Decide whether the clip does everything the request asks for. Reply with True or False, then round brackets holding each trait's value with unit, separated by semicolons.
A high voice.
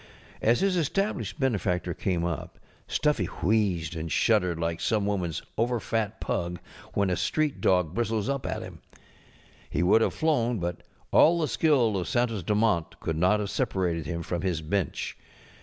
False (100 Hz)